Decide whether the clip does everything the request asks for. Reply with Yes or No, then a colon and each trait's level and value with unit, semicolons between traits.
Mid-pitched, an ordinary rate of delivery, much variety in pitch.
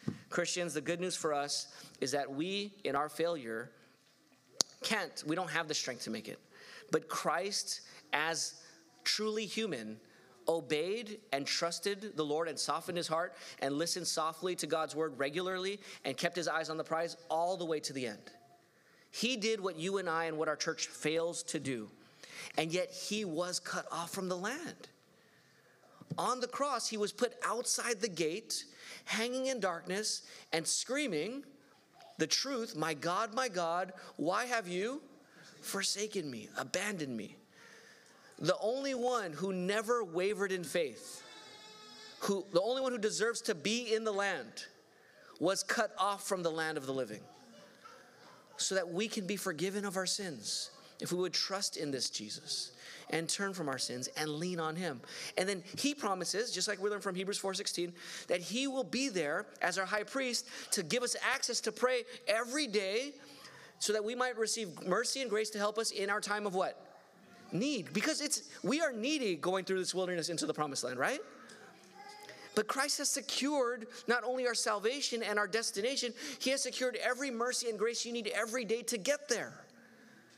No: high, 200 Hz; average, 180 wpm; wide, 6.0 semitones